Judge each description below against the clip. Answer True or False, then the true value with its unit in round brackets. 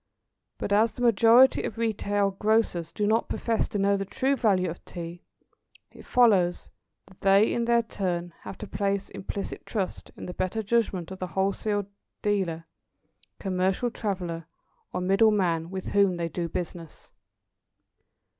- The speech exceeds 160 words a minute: False (155 wpm)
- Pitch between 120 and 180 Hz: False (195 Hz)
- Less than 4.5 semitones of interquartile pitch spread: True (3.2 semitones)